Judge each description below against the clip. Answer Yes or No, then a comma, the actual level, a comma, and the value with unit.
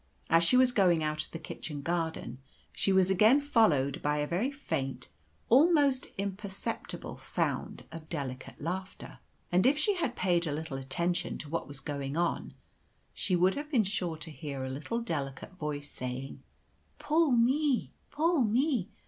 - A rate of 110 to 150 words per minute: No, average, 165 wpm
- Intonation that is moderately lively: No, wide, 8.3 semitones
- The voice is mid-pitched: Yes, medium, 175 Hz